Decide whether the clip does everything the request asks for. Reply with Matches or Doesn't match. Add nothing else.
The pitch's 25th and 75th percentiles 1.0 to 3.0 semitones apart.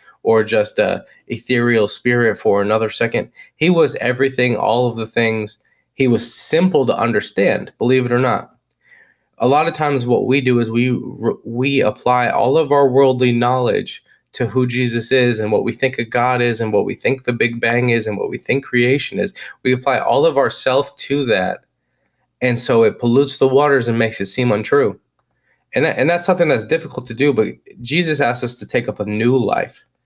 Matches